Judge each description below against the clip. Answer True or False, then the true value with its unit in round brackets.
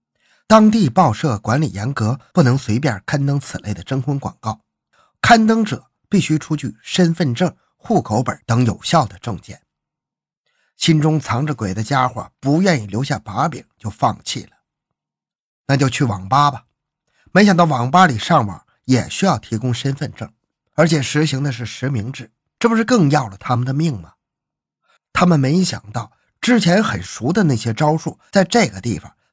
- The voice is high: False (140 Hz)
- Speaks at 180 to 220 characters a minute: False (245 characters per minute)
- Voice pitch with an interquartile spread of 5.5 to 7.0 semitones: True (6.1 semitones)